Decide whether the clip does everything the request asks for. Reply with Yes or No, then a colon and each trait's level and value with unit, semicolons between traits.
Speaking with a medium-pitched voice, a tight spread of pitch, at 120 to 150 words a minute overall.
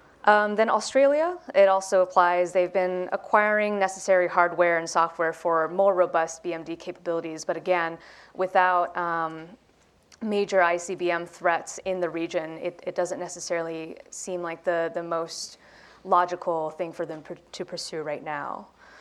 Yes: medium, 175 Hz; narrow, 2.1 semitones; average, 145 wpm